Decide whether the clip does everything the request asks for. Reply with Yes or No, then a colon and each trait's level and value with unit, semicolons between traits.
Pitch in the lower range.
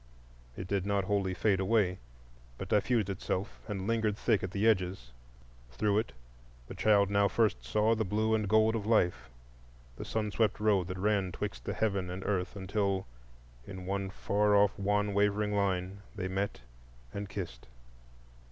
Yes: low, 100 Hz